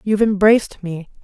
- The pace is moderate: Yes, average, 145 wpm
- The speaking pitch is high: Yes, high, 200 Hz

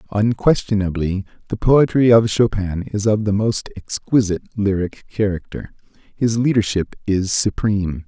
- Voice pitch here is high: No, low, 105 Hz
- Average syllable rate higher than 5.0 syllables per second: No, 4.7 syllables/s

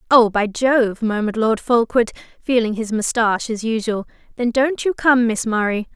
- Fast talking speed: No, average, 170 wpm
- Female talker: Yes, female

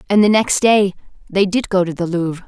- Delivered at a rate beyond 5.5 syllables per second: Yes, 5.7 syllables/s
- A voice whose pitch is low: No, high, 190 Hz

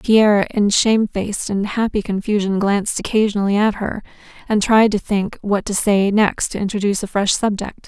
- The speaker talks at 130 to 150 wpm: No, average, 175 wpm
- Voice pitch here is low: No, high, 205 Hz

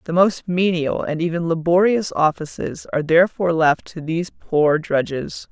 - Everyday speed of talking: Yes, average, 150 wpm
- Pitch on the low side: No, medium, 165 Hz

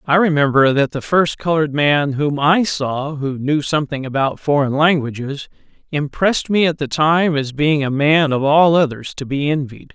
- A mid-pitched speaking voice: Yes, medium, 150 Hz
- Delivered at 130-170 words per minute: No, average, 185 wpm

